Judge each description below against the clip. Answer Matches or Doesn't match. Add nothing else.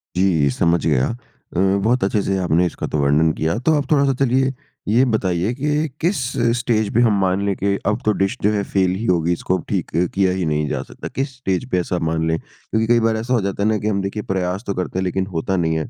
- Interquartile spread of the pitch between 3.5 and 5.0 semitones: Matches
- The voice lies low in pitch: Matches